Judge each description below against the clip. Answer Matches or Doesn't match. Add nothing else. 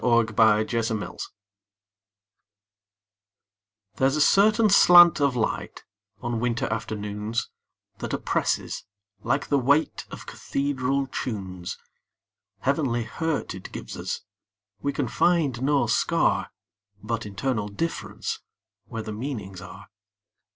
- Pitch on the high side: Doesn't match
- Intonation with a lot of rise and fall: Doesn't match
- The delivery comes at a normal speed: Doesn't match